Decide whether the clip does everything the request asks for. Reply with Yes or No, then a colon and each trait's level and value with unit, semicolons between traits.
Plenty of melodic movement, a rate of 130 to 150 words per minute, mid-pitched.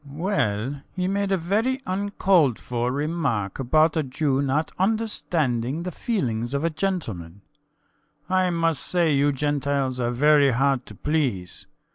Yes: wide, 5.9 semitones; average, 145 wpm; medium, 145 Hz